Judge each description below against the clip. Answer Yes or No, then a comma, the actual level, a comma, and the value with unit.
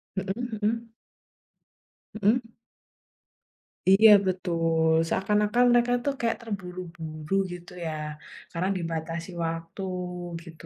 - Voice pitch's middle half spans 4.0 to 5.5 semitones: Yes, average, 4.6 semitones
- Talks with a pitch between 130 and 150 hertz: No, medium, 185 Hz